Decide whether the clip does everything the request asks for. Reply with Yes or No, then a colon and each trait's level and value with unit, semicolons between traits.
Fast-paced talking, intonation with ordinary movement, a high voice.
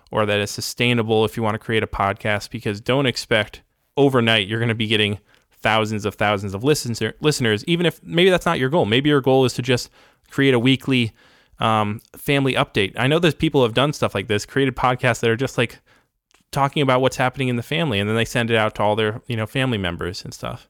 No: fast, 240 wpm; average, 3.7 semitones; low, 120 Hz